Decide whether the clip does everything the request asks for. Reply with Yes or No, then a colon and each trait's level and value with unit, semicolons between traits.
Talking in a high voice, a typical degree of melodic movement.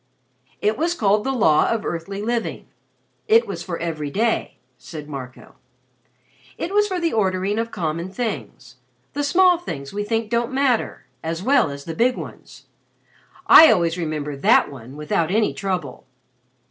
No: high, 195 Hz; wide, 7.4 semitones